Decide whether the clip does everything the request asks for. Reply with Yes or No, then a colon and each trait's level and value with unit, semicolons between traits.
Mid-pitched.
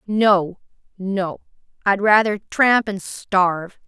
No: high, 195 Hz